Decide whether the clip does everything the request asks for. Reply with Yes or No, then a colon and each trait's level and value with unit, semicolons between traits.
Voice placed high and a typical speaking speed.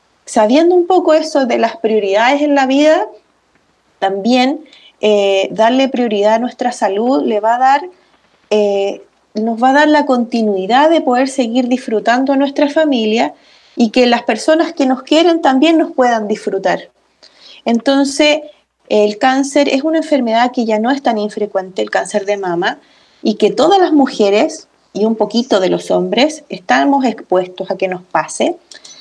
Yes: very high, 250 Hz; average, 165 wpm